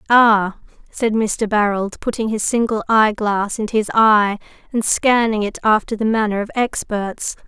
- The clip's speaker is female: Yes, female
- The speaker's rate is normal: Yes, average, 150 wpm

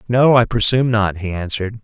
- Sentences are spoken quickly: No, average, 195 wpm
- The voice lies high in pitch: No, low, 110 Hz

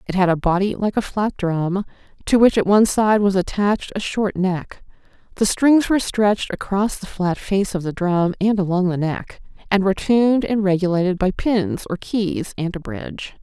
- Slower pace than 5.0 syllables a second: No, 5.1 syllables/s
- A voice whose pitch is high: Yes, high, 195 Hz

